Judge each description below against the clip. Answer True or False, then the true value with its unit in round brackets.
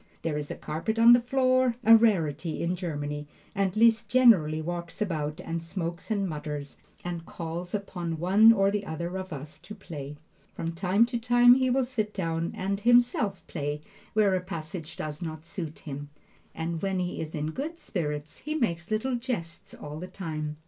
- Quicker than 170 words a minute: True (185 wpm)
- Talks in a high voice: False (175 Hz)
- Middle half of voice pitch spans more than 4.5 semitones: True (5.6 semitones)